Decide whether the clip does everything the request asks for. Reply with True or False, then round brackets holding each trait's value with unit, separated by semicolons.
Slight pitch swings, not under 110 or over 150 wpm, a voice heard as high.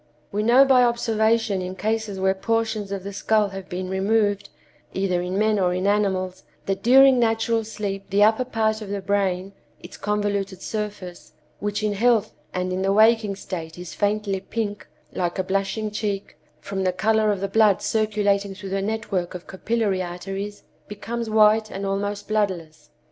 False (2.2 semitones; 165 wpm; 205 Hz)